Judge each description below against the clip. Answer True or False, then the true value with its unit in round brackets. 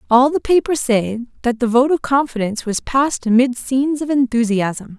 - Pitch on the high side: True (250 Hz)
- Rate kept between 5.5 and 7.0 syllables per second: False (5.3 syllables/s)